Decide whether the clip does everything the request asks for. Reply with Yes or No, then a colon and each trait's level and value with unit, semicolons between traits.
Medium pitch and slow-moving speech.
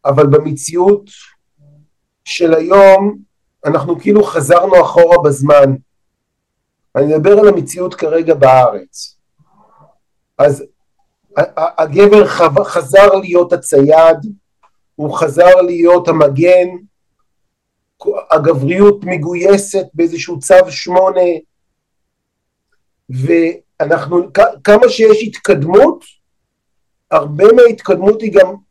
Yes: medium, 175 Hz; slow, 75 wpm